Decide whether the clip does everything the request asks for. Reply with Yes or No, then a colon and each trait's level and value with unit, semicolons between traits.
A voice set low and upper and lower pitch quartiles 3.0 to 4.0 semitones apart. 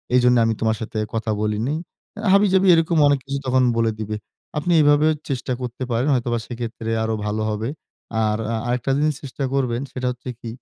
Yes: low, 125 Hz; average, 3.6 semitones